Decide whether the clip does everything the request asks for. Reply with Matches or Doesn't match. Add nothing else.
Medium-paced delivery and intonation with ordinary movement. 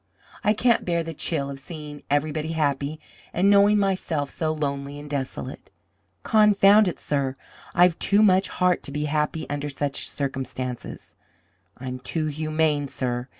Matches